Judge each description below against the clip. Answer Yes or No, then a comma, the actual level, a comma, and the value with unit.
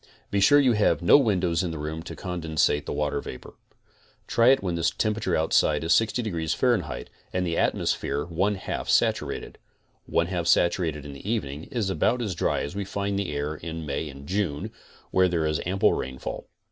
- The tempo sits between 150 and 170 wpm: No, average, 195 wpm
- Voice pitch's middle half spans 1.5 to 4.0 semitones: No, average, 4.8 semitones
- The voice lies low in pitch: Yes, very low, 85 Hz